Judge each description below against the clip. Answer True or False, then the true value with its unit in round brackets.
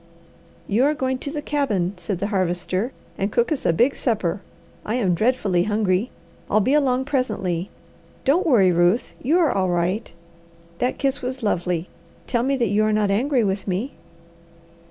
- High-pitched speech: True (215 Hz)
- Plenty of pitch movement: True (5.8 semitones)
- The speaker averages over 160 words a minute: True (175 wpm)